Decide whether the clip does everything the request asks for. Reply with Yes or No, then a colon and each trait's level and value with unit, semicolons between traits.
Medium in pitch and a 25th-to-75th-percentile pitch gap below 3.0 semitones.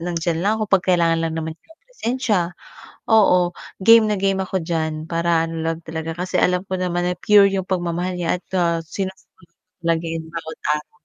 Yes: medium, 175 Hz; narrow, 2.5 semitones